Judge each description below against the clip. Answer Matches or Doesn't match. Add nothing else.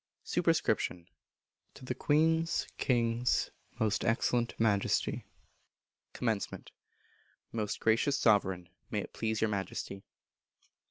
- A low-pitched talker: Matches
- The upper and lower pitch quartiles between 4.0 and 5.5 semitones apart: Doesn't match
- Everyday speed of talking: Doesn't match